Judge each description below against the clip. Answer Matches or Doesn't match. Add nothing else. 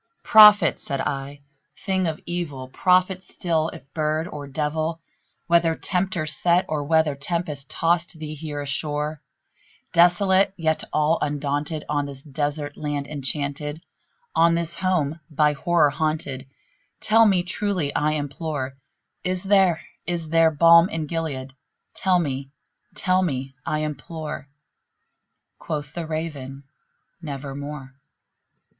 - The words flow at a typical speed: Doesn't match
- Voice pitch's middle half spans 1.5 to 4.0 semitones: Matches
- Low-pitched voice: Doesn't match